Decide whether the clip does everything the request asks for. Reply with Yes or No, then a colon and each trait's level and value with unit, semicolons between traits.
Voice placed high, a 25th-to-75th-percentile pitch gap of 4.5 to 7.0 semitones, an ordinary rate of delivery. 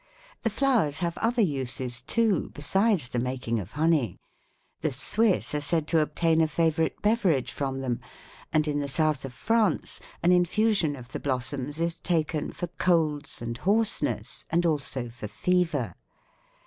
No: medium, 155 Hz; average, 5.1 semitones; average, 155 wpm